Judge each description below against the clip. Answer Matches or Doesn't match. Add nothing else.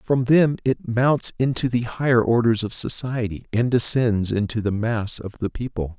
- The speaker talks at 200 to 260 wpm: Doesn't match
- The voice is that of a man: Matches